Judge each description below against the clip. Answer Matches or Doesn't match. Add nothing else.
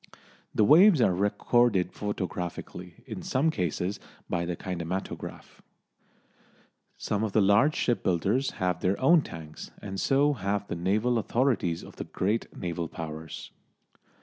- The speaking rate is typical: Doesn't match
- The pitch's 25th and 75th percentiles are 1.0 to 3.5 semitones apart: Doesn't match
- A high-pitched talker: Doesn't match